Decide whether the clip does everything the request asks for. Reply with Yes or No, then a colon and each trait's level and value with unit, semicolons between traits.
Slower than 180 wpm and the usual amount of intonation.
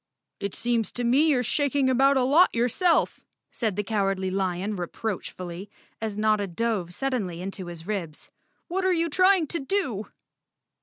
No: average, 160 wpm; wide, 6.1 semitones